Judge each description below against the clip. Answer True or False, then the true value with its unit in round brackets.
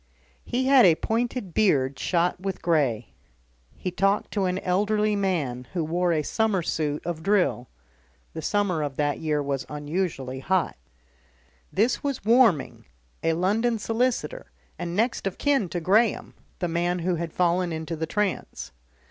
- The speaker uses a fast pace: False (155 wpm)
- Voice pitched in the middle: True (180 Hz)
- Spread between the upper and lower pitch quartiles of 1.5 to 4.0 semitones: False (4.8 semitones)